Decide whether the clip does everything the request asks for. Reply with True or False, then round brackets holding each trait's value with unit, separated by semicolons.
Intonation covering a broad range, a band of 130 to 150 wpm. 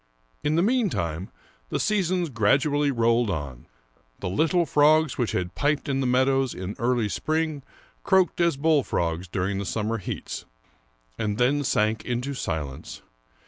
True (7.1 semitones; 140 wpm)